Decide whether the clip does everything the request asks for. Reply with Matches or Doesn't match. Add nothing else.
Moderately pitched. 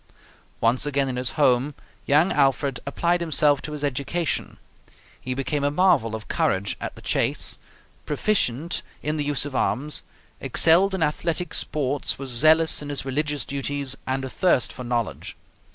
Matches